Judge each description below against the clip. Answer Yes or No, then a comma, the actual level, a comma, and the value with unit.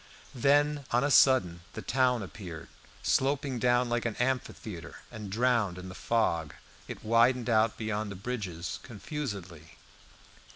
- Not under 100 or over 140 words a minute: Yes, slow, 135 wpm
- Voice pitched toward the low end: Yes, low, 115 Hz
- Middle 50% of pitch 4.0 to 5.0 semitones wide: Yes, average, 4.7 semitones